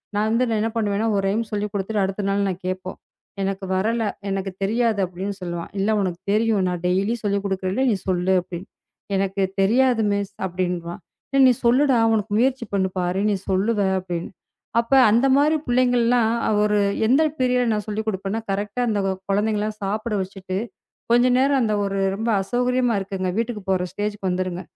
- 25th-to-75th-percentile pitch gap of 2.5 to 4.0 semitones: Yes, average, 3.3 semitones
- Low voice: No, high, 205 Hz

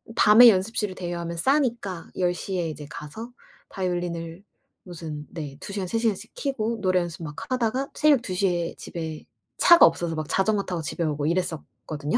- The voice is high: No, medium, 180 Hz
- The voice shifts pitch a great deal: No, average, 4.7 semitones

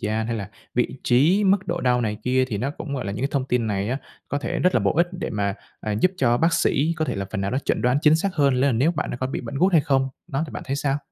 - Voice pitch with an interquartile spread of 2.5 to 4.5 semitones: No, average, 5.0 semitones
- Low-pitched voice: Yes, low, 130 Hz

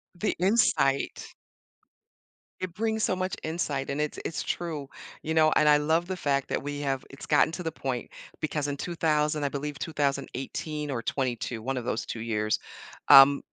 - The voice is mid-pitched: Yes, medium, 150 Hz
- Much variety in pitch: No, average, 3.0 semitones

